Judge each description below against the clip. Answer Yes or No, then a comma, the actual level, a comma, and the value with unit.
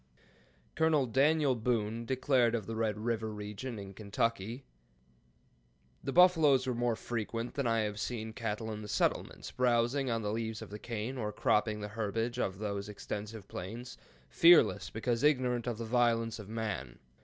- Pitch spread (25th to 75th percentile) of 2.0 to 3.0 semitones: Yes, average, 2.7 semitones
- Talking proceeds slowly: No, average, 165 wpm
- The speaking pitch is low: Yes, low, 115 Hz